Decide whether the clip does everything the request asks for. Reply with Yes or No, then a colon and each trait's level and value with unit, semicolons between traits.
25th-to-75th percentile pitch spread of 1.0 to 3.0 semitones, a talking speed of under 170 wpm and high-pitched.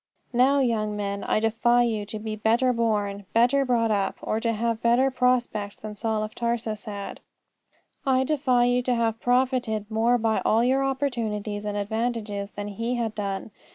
No: narrow, 2.6 semitones; average, 175 wpm; high, 225 Hz